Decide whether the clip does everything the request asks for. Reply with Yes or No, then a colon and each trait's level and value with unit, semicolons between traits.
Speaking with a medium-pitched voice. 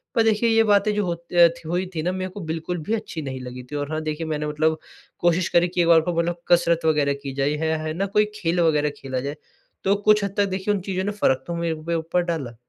Yes: medium, 170 Hz